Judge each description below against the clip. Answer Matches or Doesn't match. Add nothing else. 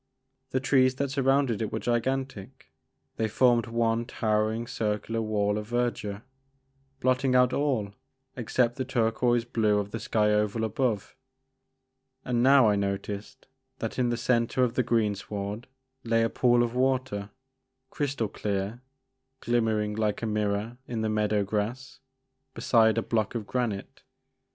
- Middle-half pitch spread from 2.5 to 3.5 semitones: Matches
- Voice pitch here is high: Doesn't match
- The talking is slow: Doesn't match